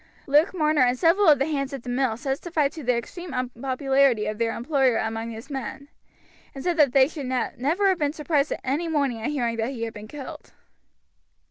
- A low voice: No, very high, 270 Hz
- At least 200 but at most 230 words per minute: Yes, fast, 205 wpm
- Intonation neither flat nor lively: Yes, average, 3.6 semitones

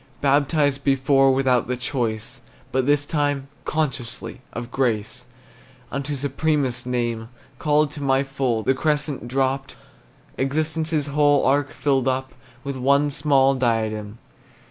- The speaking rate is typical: No, slow, 120 wpm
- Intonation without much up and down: Yes, narrow, 2.3 semitones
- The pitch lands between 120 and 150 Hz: Yes, low, 135 Hz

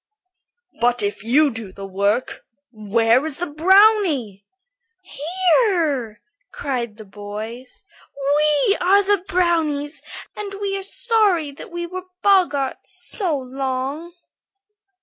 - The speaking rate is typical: No, slow, 110 wpm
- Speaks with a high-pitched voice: Yes, very high, 290 Hz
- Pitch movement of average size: No, wide, 7.5 semitones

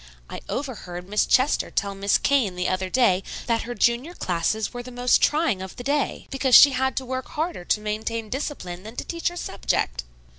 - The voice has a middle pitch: No, high, 240 Hz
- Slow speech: No, average, 200 wpm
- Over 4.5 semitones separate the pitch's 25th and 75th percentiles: Yes, average, 5.3 semitones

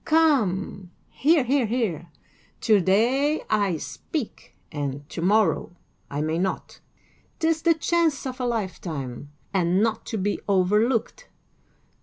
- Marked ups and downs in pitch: Yes, wide, 7.1 semitones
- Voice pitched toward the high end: Yes, high, 210 Hz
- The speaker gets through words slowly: Yes, slow, 125 wpm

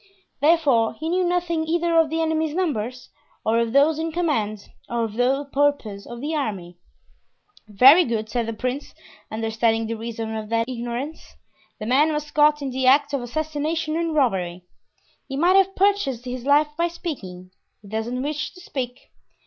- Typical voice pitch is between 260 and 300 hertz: Yes, very high, 270 Hz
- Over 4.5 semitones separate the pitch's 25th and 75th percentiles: Yes, wide, 5.6 semitones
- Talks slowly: No, average, 175 wpm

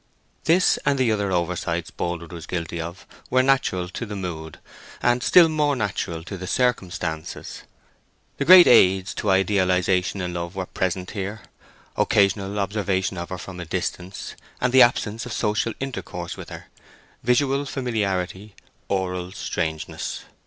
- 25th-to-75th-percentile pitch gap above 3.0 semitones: Yes, average, 4.7 semitones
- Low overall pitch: Yes, very low, 95 Hz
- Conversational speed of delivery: Yes, average, 145 wpm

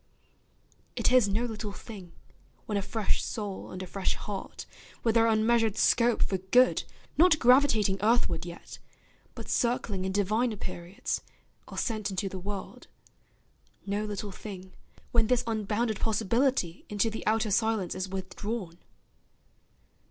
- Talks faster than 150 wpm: No, slow, 135 wpm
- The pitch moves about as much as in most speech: Yes, average, 3.1 semitones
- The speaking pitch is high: Yes, high, 210 Hz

